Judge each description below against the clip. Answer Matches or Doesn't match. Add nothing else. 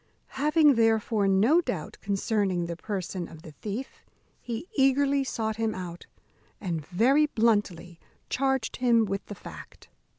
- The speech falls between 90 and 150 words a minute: Matches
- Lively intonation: Matches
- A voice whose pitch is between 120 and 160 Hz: Doesn't match